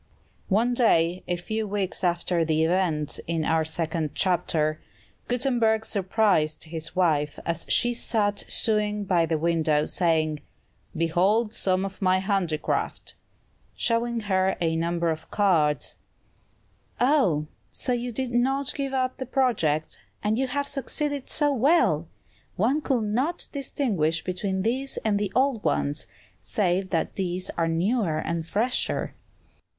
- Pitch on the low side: No, high, 190 Hz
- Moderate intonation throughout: No, wide, 6.3 semitones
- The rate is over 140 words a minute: No, slow, 135 wpm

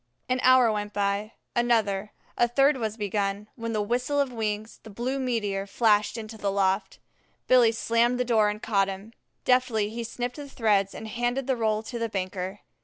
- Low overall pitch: No, high, 220 Hz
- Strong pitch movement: No, average, 2.8 semitones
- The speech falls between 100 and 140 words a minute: No, average, 190 wpm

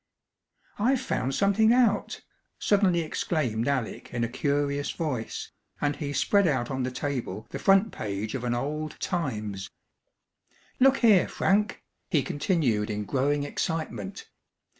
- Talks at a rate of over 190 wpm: No, slow, 135 wpm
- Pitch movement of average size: No, wide, 7.6 semitones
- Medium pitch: Yes, medium, 145 Hz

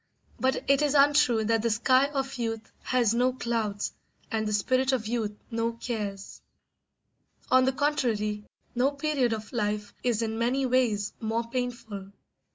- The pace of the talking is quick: No, average, 155 wpm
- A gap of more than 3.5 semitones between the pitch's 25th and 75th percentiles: No, average, 3.1 semitones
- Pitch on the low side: No, high, 235 Hz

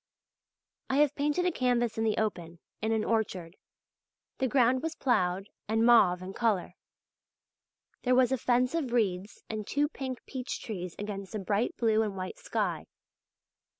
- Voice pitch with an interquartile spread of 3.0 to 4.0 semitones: No, average, 4.4 semitones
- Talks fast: No, average, 160 wpm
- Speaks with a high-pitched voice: Yes, high, 225 Hz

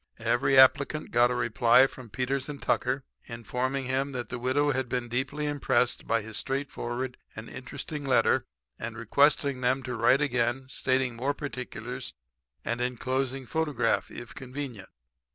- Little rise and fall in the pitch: Yes, narrow, 2.2 semitones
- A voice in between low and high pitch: No, low, 130 Hz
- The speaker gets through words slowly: No, average, 150 wpm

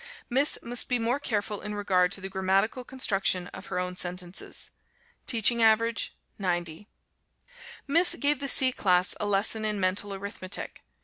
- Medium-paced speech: Yes, average, 150 wpm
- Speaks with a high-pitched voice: Yes, high, 205 Hz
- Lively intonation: No, average, 4.0 semitones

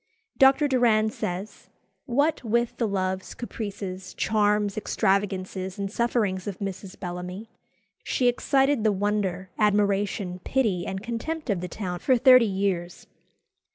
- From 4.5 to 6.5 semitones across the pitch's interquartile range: No, average, 3.9 semitones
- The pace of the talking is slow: Yes, slow, 125 wpm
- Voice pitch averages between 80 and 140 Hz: No, high, 205 Hz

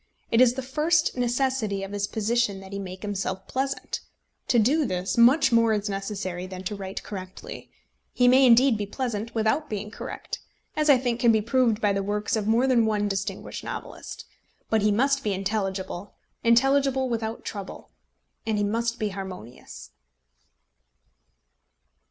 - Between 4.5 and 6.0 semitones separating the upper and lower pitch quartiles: No, average, 3.8 semitones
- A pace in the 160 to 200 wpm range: Yes, average, 165 wpm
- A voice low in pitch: No, high, 220 Hz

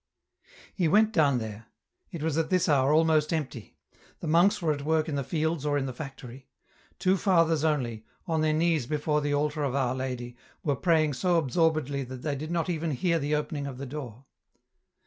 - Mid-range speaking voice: Yes, medium, 150 Hz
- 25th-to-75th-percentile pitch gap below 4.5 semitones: Yes, average, 3.1 semitones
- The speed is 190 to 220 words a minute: Yes, average, 200 wpm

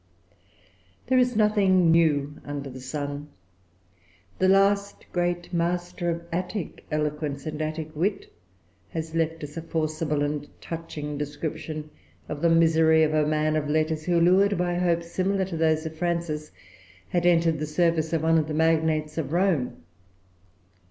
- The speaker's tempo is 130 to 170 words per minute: Yes, average, 150 wpm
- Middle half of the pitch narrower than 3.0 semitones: Yes, narrow, 2.4 semitones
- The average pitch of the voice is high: No, medium, 160 Hz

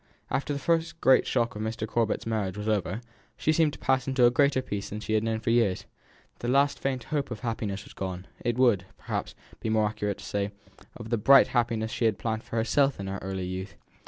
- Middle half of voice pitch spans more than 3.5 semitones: Yes, average, 4.0 semitones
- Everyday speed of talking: No, fast, 230 wpm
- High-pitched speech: No, low, 115 Hz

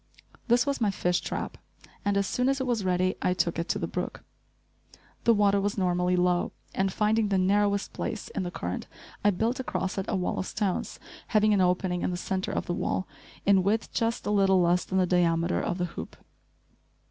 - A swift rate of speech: Yes, fast, 210 wpm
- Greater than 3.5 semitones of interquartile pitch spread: No, narrow, 2.6 semitones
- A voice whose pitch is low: No, high, 190 Hz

